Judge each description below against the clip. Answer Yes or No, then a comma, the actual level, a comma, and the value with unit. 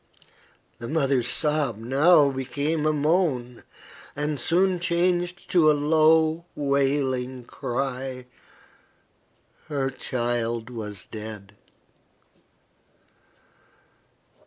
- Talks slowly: Yes, slow, 80 wpm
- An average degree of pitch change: Yes, average, 4.1 semitones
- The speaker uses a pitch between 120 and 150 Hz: Yes, medium, 140 Hz